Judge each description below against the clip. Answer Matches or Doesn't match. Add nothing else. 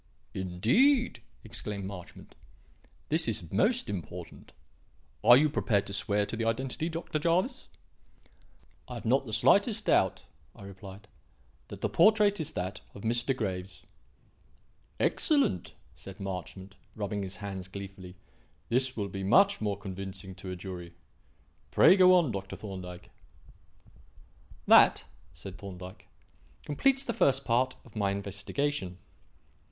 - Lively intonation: Matches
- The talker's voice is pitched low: Matches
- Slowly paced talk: Matches